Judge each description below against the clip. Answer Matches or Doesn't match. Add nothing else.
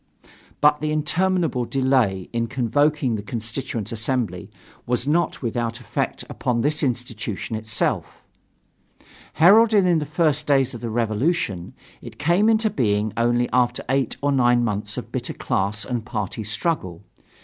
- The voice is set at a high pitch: Doesn't match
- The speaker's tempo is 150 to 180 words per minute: Doesn't match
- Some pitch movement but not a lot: Matches